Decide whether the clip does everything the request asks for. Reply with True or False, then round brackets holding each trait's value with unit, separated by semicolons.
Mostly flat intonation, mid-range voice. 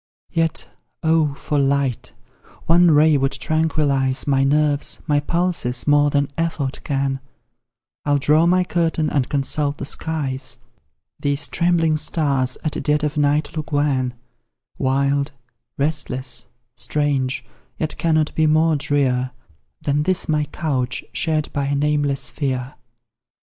True (2.3 semitones; 145 Hz)